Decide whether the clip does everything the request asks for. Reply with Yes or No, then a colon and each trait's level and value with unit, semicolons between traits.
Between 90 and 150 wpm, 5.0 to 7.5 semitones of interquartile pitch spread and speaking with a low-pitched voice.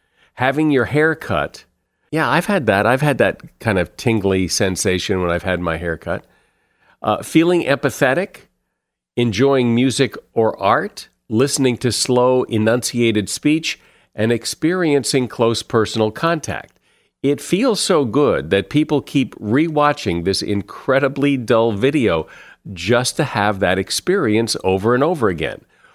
Yes: average, 140 wpm; wide, 5.6 semitones; low, 125 Hz